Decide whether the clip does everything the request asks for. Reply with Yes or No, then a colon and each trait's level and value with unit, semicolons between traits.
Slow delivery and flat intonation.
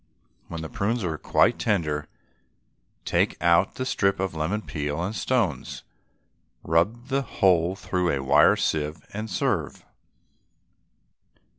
No: slow, 125 wpm; average, 5.2 semitones